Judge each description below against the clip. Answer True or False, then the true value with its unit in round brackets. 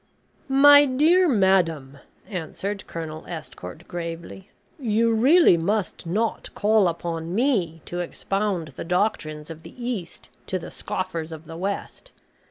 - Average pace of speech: False (130 wpm)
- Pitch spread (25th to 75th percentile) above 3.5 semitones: True (5.2 semitones)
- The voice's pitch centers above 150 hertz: True (185 Hz)